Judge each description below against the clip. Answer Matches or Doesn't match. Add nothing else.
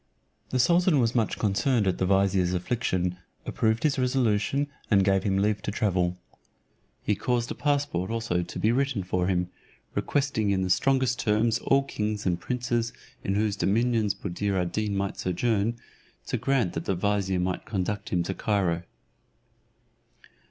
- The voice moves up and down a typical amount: Matches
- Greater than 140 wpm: Matches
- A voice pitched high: Doesn't match